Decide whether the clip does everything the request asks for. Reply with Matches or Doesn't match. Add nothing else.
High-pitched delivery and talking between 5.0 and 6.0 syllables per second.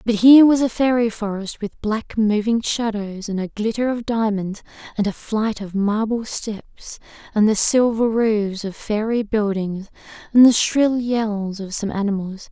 Doesn't match